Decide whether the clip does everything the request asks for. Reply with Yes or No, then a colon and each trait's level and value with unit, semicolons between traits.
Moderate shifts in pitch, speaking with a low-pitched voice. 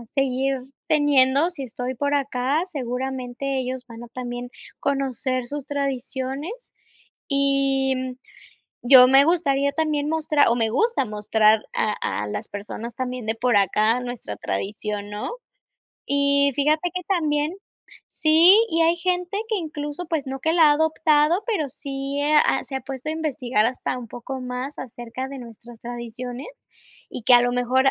No: average, 3.3 semitones; very high, 270 Hz